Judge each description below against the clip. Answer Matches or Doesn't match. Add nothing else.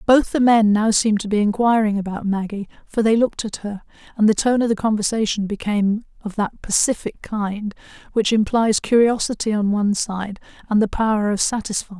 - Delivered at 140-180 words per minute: Doesn't match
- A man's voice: Doesn't match